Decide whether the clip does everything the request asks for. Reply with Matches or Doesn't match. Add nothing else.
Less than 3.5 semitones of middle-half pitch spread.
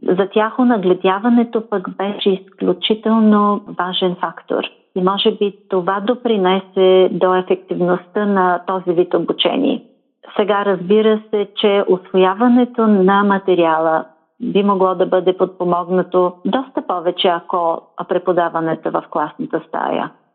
Matches